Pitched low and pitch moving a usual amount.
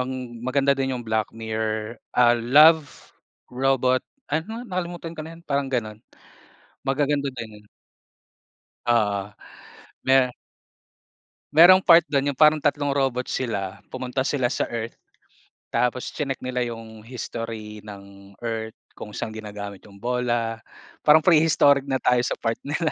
Yes: low, 125 Hz; average, 4.2 semitones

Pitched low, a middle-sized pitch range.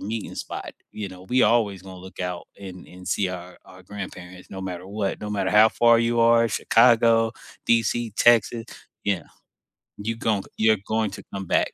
Yes: low, 105 Hz; average, 3.5 semitones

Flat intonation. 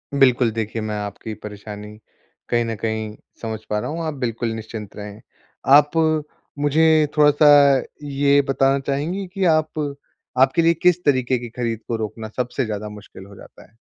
No: average, 5.0 semitones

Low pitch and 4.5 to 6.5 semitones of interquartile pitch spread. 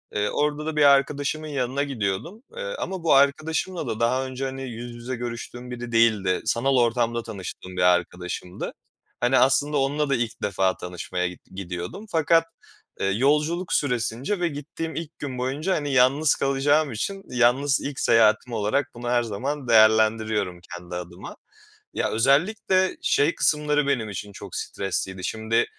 Yes: low, 125 Hz; average, 5.0 semitones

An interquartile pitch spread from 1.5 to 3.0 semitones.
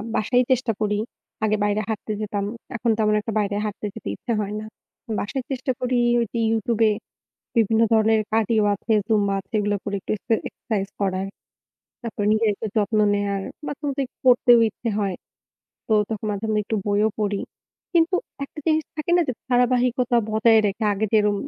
Yes: average, 2.7 semitones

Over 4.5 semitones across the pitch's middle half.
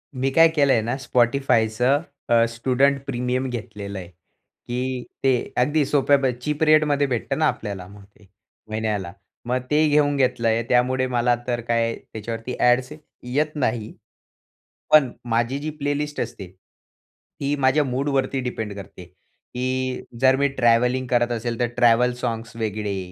No: average, 3.0 semitones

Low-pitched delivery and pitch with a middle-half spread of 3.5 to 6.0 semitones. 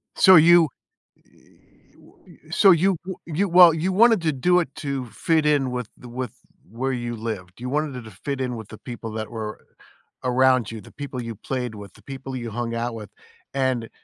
Yes: low, 130 Hz; average, 5.1 semitones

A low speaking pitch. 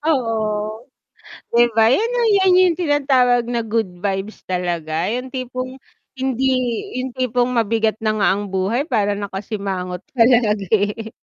No: high, 225 Hz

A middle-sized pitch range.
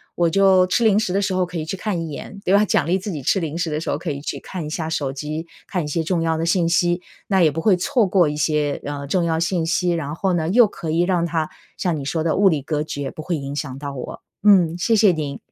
Yes: average, 3.3 semitones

